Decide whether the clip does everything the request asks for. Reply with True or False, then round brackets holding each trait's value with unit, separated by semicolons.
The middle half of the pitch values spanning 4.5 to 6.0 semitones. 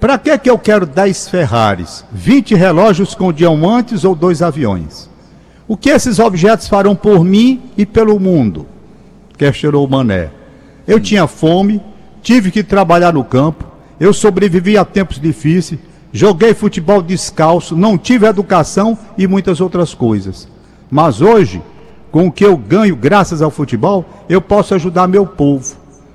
False (3.9 semitones)